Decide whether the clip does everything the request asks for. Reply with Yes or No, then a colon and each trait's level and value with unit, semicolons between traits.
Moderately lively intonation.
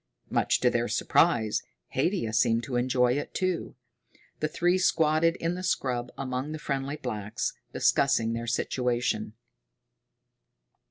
Yes: average, 4.9 semitones